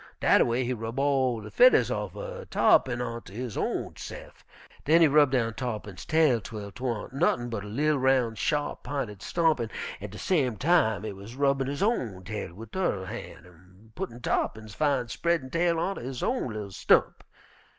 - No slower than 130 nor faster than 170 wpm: No, average, 185 wpm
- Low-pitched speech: Yes, low, 125 Hz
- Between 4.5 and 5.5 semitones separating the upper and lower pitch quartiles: Yes, average, 5.2 semitones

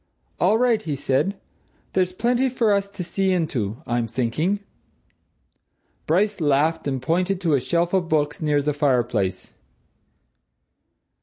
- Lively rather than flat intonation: Yes, wide, 6.2 semitones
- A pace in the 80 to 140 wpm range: Yes, slow, 135 wpm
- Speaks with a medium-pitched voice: Yes, medium, 165 Hz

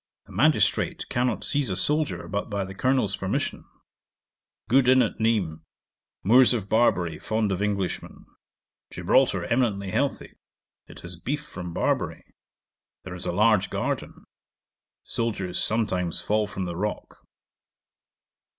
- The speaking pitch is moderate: No, low, 105 Hz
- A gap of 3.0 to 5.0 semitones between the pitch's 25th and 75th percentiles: Yes, average, 4.4 semitones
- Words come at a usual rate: No, slow, 130 wpm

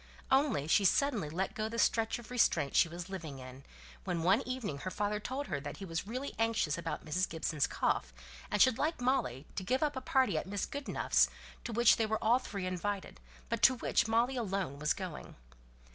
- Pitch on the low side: No, high, 205 Hz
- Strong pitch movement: Yes, wide, 6.7 semitones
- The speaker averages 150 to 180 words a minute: No, fast, 205 wpm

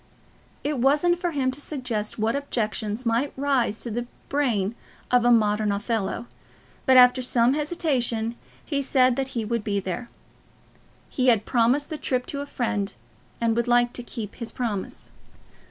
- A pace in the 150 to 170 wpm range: Yes, average, 165 wpm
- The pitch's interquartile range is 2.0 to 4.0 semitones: Yes, average, 3.3 semitones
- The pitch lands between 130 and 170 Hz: No, high, 245 Hz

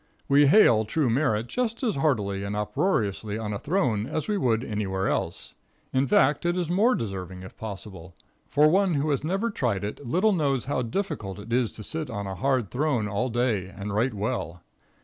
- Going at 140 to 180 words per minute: No, average, 195 wpm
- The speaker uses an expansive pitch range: Yes, wide, 6.8 semitones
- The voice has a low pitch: Yes, low, 120 Hz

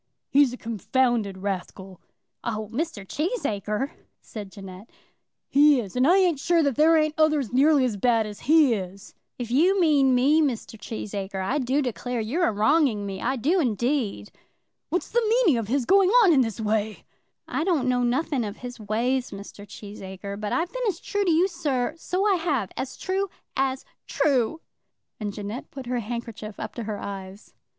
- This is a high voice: Yes, very high, 250 Hz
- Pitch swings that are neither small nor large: No, wide, 6.5 semitones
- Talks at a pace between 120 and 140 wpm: No, average, 180 wpm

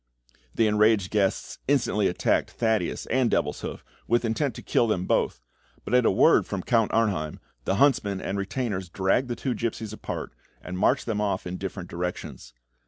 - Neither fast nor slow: Yes, average, 170 wpm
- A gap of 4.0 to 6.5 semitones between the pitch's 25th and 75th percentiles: No, average, 3.6 semitones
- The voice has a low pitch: Yes, low, 105 Hz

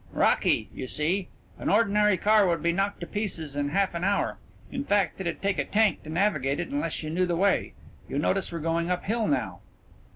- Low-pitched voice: No, medium, 185 Hz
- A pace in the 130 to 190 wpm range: No, fast, 205 wpm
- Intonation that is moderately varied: Yes, average, 3.7 semitones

